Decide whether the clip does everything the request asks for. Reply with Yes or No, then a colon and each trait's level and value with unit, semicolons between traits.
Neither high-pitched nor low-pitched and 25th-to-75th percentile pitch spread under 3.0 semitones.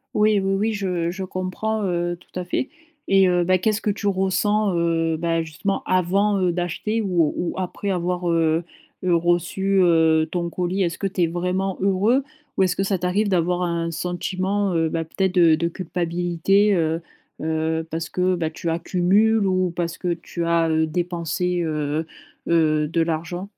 Yes: medium, 175 Hz; narrow, 2.4 semitones